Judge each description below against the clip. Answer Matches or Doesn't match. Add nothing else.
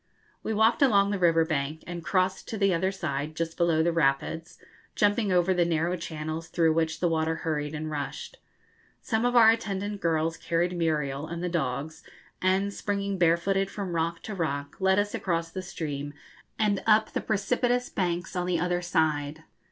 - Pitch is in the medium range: Matches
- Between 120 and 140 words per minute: Doesn't match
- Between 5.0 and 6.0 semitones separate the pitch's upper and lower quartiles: Doesn't match